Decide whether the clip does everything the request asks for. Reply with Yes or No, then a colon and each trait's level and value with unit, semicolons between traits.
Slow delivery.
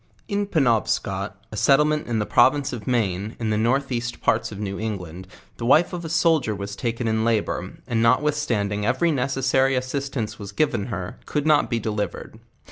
No: average, 185 wpm